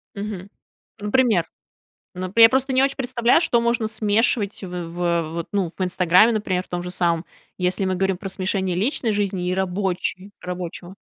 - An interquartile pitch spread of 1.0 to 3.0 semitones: No, average, 3.4 semitones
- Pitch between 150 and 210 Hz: Yes, high, 190 Hz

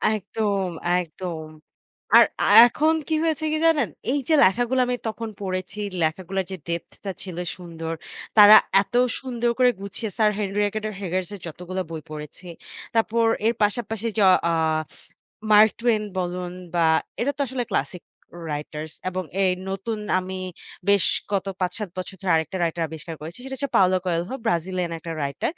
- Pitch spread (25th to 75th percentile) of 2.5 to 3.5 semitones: No, average, 4.3 semitones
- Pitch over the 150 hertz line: Yes, high, 190 Hz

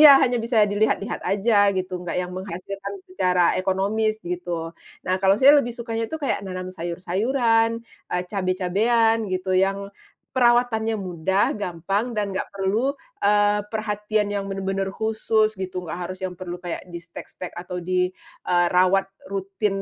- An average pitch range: Yes, average, 3.2 semitones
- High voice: Yes, high, 195 Hz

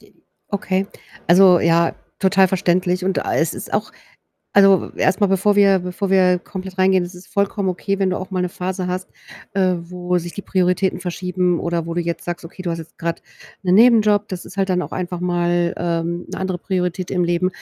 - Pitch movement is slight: Yes, narrow, 1.6 semitones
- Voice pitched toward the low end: No, medium, 185 Hz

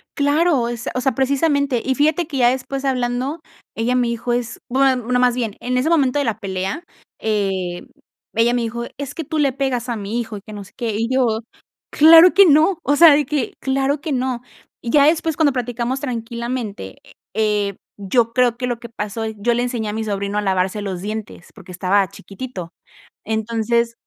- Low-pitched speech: No, high, 240 Hz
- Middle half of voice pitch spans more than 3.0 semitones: Yes, average, 3.7 semitones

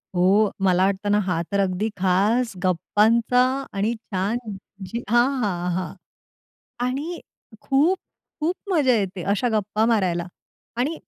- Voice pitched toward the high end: Yes, high, 210 Hz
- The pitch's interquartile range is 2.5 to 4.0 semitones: No, average, 4.5 semitones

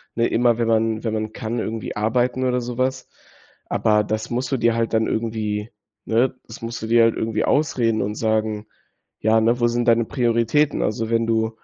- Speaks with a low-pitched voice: Yes, low, 115 Hz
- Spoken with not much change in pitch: Yes, narrow, 1.4 semitones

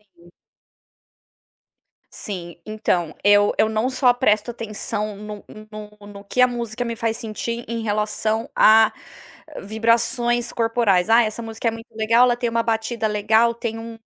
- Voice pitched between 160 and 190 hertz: No, high, 225 Hz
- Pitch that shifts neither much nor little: No, narrow, 1.7 semitones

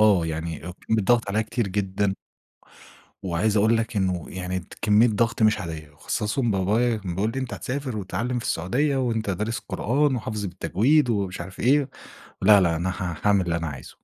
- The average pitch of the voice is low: Yes, low, 105 Hz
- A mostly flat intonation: No, average, 4.1 semitones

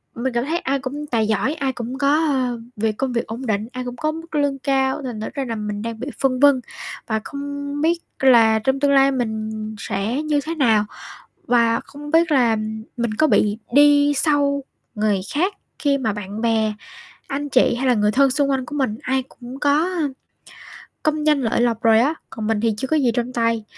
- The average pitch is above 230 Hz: Yes, very high, 260 Hz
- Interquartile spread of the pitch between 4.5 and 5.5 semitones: No, average, 4.0 semitones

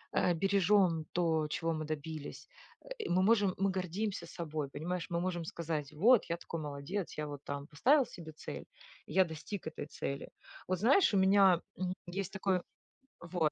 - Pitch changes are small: No, average, 3.6 semitones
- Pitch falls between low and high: Yes, medium, 175 Hz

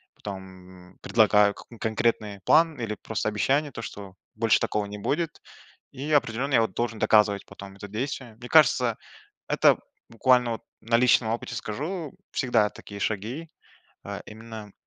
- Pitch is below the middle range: Yes, low, 110 Hz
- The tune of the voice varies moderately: Yes, average, 3.6 semitones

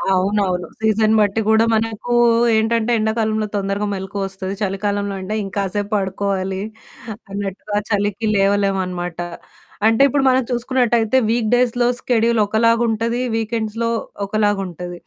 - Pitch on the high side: Yes, high, 210 Hz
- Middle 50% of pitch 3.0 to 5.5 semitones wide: No, narrow, 2.5 semitones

